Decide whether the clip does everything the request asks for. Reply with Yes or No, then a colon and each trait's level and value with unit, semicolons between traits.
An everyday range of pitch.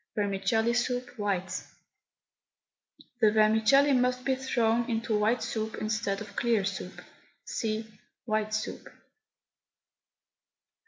No: narrow, 2.3 semitones